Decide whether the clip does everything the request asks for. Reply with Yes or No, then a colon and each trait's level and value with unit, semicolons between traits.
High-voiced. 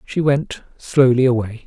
No: low, 130 Hz